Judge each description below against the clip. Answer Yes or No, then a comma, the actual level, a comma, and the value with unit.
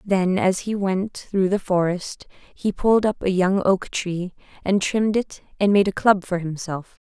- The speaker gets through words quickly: No, average, 195 wpm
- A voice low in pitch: No, high, 190 Hz